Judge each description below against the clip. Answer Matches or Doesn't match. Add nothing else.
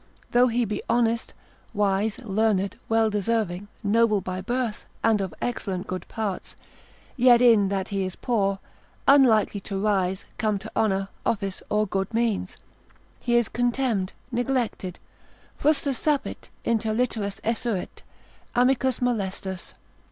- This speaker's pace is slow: Matches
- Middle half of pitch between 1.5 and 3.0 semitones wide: Doesn't match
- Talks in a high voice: Matches